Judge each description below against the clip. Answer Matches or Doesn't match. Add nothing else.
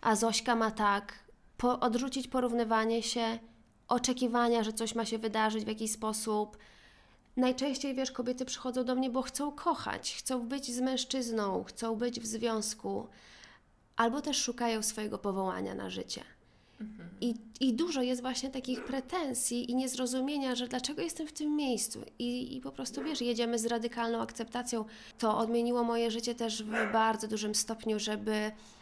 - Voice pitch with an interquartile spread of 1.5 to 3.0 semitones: Matches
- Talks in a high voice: Matches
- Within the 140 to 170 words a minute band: Matches